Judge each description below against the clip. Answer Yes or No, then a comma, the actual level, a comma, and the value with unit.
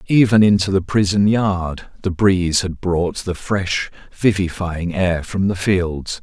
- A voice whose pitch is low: Yes, very low, 95 Hz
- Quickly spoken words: No, average, 155 wpm